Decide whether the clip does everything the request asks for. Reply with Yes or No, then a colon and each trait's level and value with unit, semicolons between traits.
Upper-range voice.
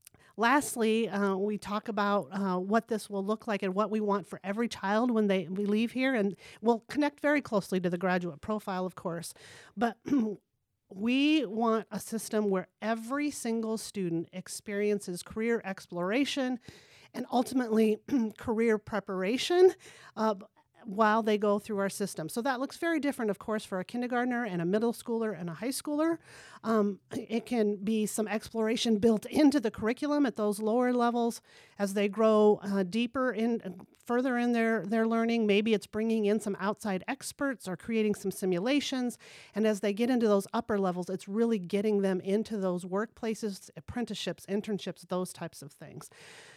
Yes: high, 215 Hz